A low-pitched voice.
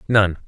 Yes: low, 100 Hz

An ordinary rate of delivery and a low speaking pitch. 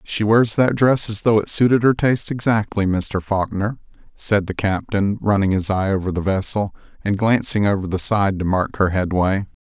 Yes: average, 195 wpm; low, 100 Hz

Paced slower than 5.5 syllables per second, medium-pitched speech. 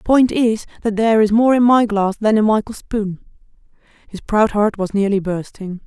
No: 5.2 syllables/s; high, 215 Hz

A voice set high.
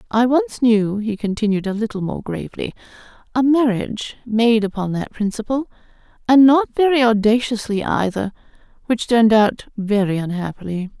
Yes: high, 225 Hz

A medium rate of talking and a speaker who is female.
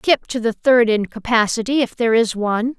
Yes: average, 195 wpm; female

